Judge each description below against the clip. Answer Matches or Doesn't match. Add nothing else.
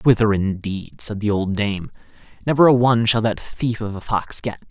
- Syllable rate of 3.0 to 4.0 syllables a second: Doesn't match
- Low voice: Matches